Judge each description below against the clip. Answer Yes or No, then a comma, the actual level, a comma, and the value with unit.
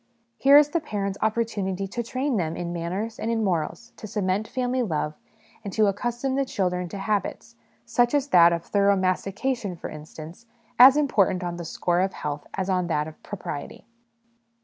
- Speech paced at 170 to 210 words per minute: Yes, average, 180 wpm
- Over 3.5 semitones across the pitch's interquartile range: Yes, average, 4.9 semitones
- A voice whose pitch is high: Yes, high, 200 Hz